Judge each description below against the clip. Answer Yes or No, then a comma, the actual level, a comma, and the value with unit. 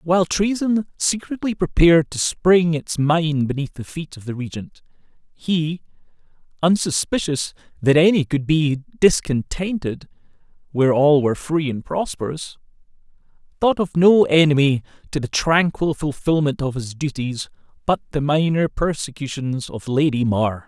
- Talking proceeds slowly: Yes, slow, 130 wpm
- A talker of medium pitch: Yes, medium, 155 Hz